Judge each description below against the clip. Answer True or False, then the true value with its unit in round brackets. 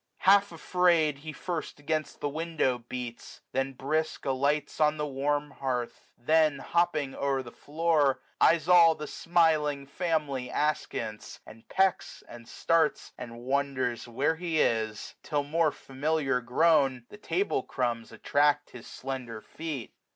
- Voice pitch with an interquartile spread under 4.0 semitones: True (3.6 semitones)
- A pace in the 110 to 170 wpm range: True (145 wpm)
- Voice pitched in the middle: True (145 Hz)